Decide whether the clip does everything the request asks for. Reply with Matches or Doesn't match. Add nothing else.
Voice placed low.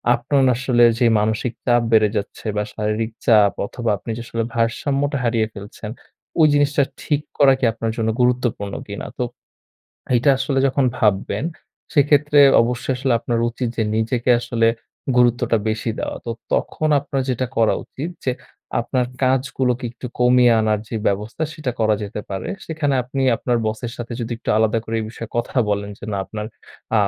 Matches